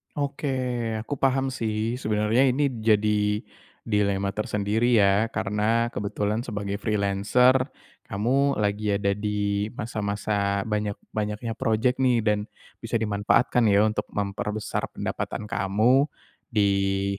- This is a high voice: No, low, 105 Hz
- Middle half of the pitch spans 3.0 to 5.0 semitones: No, narrow, 2.4 semitones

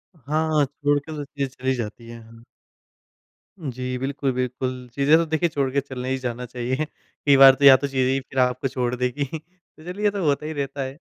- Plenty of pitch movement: No, narrow, 2.5 semitones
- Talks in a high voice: No, low, 135 Hz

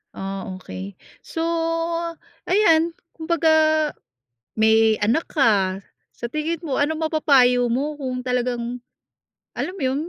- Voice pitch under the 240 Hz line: No, very high, 265 Hz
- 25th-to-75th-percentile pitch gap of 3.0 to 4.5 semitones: No, wide, 5.6 semitones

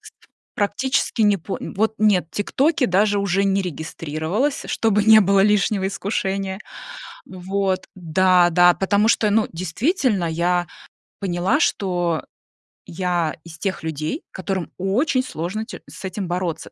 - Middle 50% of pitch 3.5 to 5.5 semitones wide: No, average, 3.1 semitones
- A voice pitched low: No, high, 190 Hz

